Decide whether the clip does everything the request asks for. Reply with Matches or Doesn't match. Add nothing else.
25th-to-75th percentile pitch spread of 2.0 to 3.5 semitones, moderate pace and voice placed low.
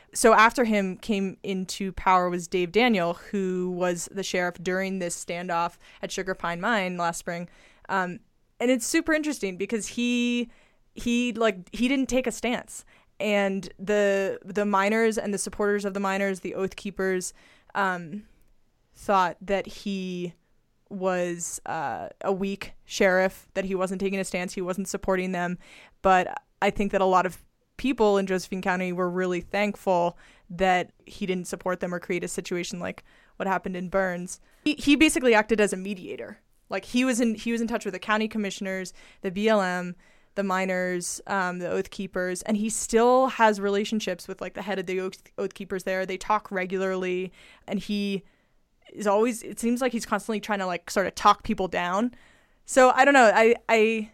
Doesn't match